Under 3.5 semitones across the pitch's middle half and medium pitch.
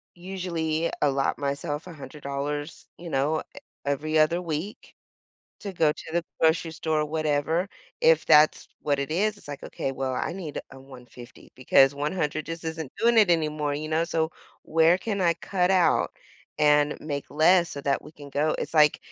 Yes: average, 2.7 semitones; medium, 155 Hz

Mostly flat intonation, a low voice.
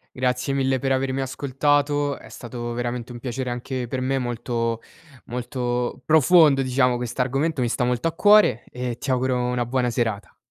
Yes: narrow, 1.8 semitones; low, 125 Hz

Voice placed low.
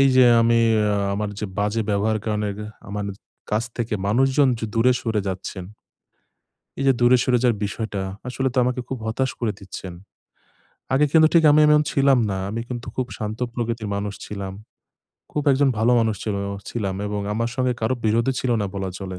Yes: low, 115 Hz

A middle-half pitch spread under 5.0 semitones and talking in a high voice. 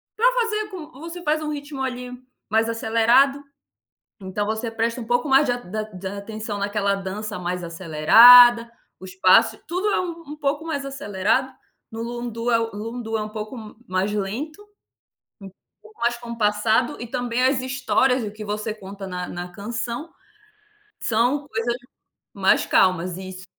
Yes: average, 4.5 semitones; high, 230 Hz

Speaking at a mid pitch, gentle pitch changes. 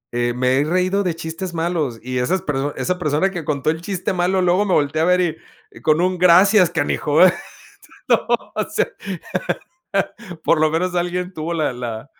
No: medium, 165 Hz; average, 3.5 semitones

